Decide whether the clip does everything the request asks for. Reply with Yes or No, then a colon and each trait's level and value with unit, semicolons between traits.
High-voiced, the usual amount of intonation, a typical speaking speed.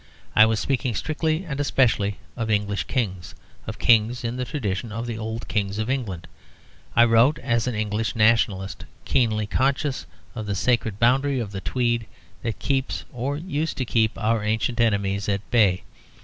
No: low, 115 Hz; average, 3.3 semitones; average, 170 wpm